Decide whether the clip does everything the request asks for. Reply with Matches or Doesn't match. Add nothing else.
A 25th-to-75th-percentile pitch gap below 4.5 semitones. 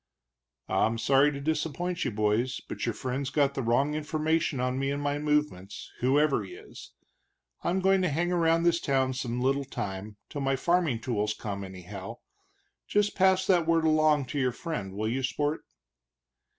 Doesn't match